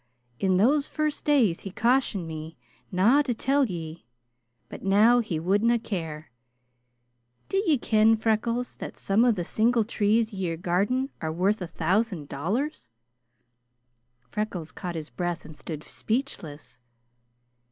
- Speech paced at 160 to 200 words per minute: No, slow, 135 wpm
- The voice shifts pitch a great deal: Yes, wide, 5.8 semitones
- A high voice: Yes, high, 205 Hz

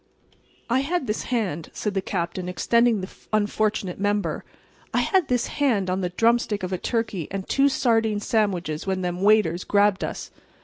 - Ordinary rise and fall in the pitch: Yes, average, 3.8 semitones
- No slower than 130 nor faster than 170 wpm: Yes, average, 165 wpm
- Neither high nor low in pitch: No, high, 205 Hz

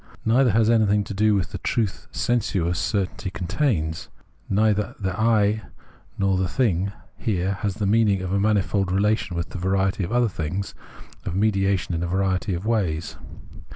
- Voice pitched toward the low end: Yes, low, 100 Hz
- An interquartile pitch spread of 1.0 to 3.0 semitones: Yes, average, 2.7 semitones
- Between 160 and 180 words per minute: Yes, average, 165 wpm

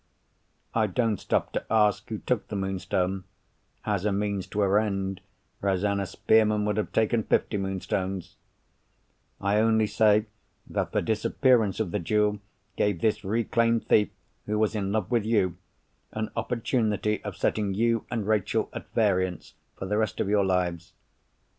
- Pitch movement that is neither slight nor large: No, narrow, 2.1 semitones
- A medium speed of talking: Yes, average, 155 wpm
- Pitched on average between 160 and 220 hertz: No, low, 105 Hz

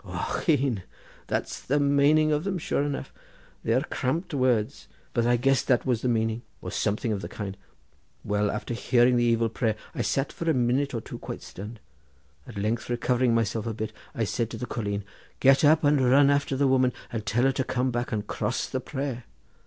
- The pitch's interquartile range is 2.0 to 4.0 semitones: Yes, average, 3.4 semitones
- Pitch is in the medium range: No, low, 125 Hz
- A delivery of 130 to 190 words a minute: No, fast, 205 wpm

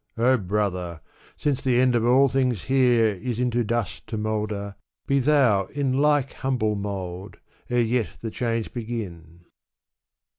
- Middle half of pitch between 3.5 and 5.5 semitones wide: Yes, average, 3.9 semitones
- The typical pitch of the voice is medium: No, low, 115 Hz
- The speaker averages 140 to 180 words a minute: Yes, average, 145 wpm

